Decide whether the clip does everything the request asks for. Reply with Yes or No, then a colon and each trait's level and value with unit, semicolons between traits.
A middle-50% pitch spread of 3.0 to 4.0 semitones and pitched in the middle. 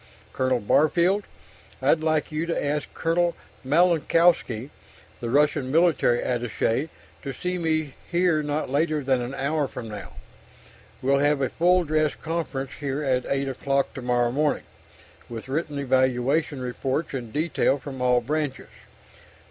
Yes: average, 3.3 semitones; medium, 145 Hz